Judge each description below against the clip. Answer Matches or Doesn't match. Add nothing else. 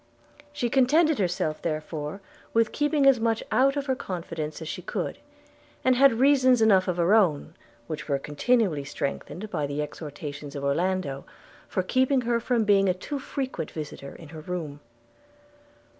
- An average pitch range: Doesn't match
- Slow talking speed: Doesn't match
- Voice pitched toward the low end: Doesn't match